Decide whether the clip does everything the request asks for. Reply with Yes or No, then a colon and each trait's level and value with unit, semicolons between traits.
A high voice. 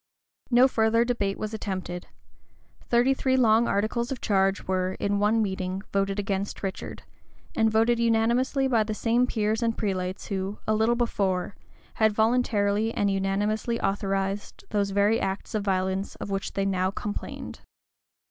Yes: high, 210 Hz